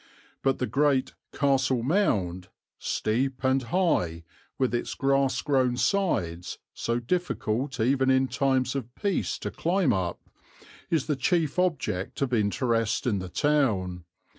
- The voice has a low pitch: Yes, low, 130 Hz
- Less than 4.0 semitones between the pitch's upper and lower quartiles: No, average, 4.3 semitones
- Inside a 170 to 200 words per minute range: No, slow, 135 wpm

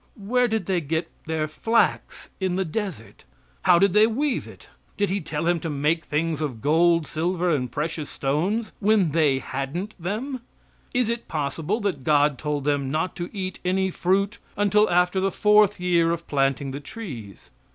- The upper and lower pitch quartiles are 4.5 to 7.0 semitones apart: Yes, average, 5.1 semitones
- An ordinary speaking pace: Yes, average, 175 wpm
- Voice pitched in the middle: Yes, medium, 170 Hz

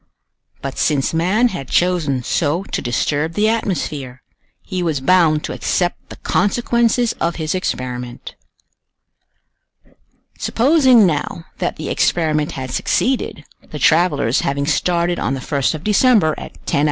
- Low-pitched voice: No, medium, 165 Hz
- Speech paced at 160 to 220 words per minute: No, slow, 135 wpm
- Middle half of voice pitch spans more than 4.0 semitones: Yes, wide, 5.5 semitones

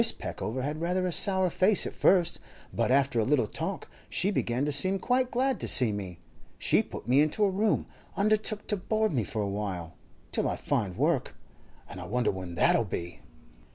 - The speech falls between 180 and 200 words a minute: Yes, average, 190 wpm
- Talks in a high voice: No, medium, 145 Hz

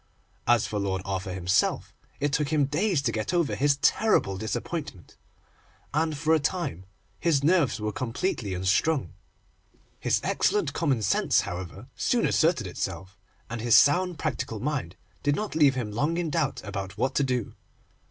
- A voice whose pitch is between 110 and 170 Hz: Yes, low, 135 Hz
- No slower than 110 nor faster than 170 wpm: Yes, average, 160 wpm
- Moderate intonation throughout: No, wide, 7.5 semitones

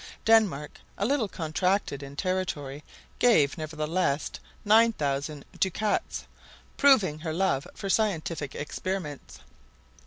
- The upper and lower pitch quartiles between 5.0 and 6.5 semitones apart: Yes, wide, 5.5 semitones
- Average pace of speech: No, slow, 95 wpm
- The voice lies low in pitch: No, medium, 170 Hz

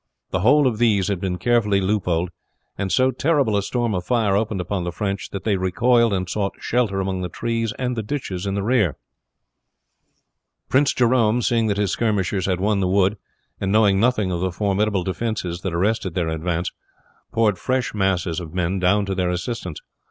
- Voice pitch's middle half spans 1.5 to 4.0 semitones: Yes, average, 3.6 semitones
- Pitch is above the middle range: No, low, 100 Hz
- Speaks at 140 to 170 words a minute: No, average, 185 wpm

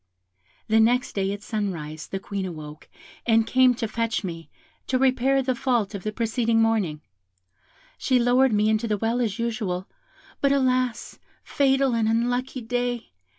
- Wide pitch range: No, average, 3.4 semitones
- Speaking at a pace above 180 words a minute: No, average, 155 wpm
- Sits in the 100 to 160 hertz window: No, high, 230 Hz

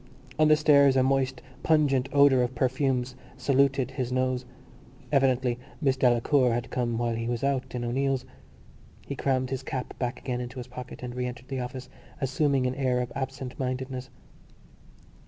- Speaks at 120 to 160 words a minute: No, average, 170 wpm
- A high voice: No, low, 130 Hz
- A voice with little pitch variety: Yes, narrow, 1.5 semitones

